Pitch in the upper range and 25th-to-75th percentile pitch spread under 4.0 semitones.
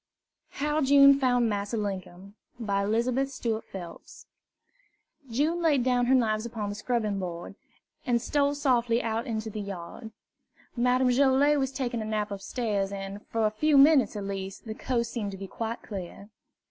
No: high, 230 Hz; average, 4.3 semitones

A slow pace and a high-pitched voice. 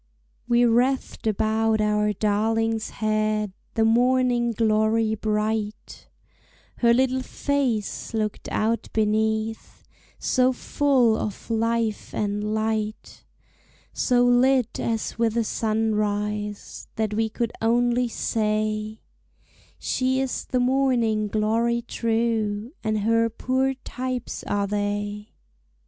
Yes: slow, 105 wpm; high, 225 Hz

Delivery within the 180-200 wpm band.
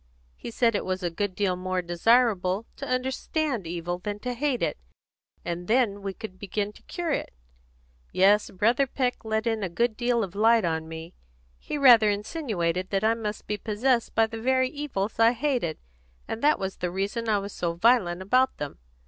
Yes: average, 190 wpm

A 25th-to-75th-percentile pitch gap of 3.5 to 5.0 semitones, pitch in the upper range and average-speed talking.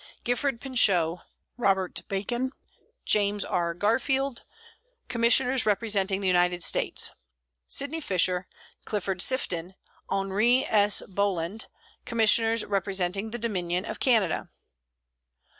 No: average, 4.1 semitones; high, 205 Hz; slow, 95 wpm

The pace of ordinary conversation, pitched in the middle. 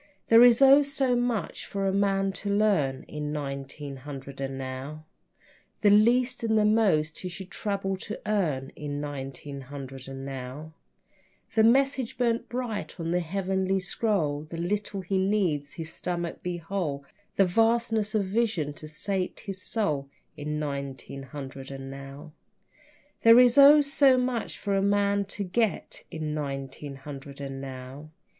Yes: average, 160 wpm; medium, 180 Hz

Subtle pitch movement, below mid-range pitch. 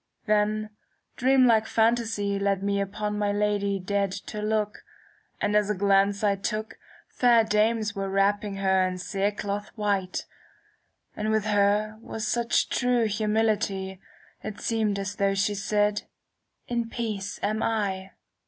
No: narrow, 1.6 semitones; high, 210 Hz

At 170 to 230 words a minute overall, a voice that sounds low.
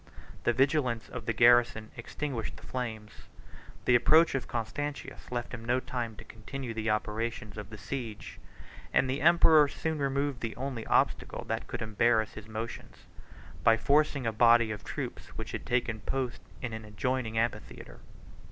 No: average, 160 wpm; low, 120 Hz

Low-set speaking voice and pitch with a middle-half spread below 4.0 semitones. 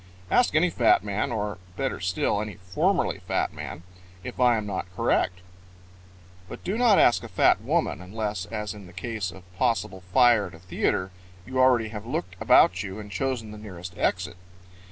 No: low, 105 Hz; average, 4.3 semitones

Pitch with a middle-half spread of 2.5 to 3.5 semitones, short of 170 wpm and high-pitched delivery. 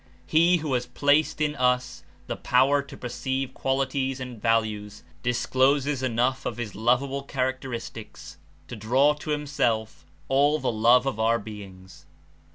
No: average, 3.2 semitones; average, 145 wpm; low, 130 Hz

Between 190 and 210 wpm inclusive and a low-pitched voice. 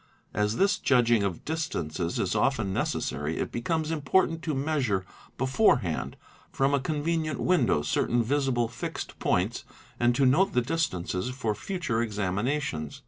No: average, 140 wpm; low, 125 Hz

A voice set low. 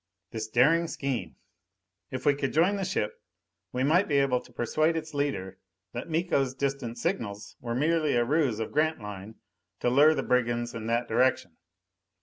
Yes: low, 130 Hz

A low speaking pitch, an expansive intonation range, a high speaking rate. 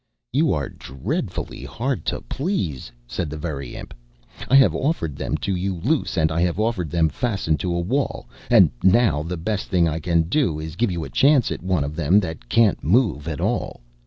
Yes: very low, 85 Hz; wide, 6.1 semitones; fast, 210 wpm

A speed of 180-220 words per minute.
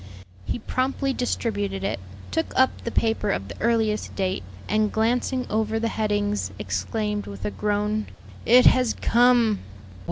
No: average, 140 wpm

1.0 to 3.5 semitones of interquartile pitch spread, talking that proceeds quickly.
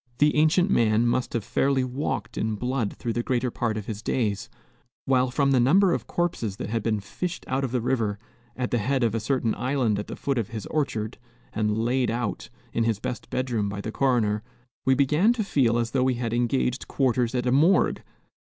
Yes: average, 3.1 semitones; fast, 215 wpm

